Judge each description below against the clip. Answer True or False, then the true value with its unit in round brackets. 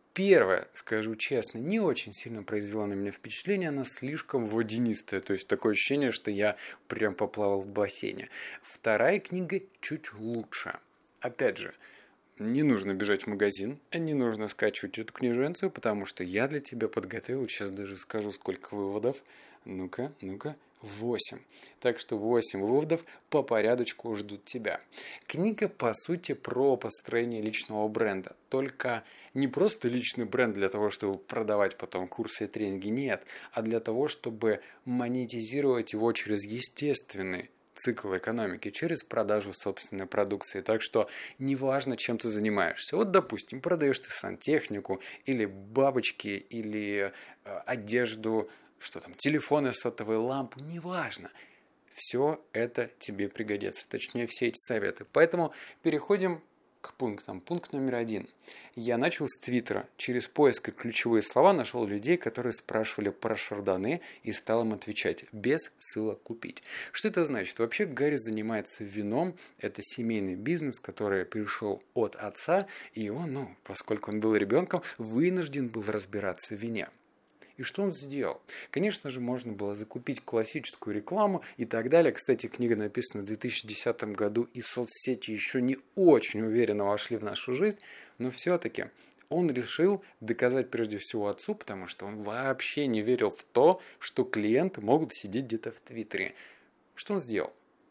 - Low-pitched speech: True (115 Hz)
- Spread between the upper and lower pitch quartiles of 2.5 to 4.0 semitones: False (4.4 semitones)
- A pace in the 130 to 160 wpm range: True (145 wpm)